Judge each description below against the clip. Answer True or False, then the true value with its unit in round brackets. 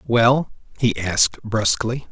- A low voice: True (115 Hz)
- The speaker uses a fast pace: False (115 wpm)